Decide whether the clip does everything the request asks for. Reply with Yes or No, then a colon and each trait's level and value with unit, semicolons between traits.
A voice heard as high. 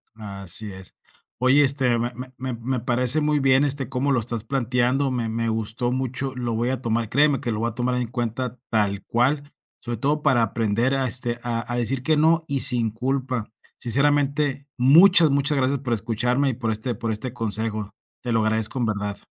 No: low, 125 Hz